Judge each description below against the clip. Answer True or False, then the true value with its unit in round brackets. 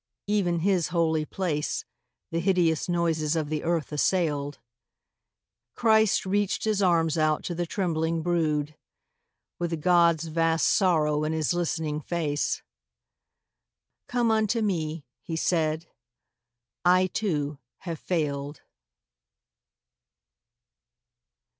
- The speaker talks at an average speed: False (105 wpm)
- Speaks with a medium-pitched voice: True (165 Hz)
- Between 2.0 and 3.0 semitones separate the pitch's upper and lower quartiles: True (2.7 semitones)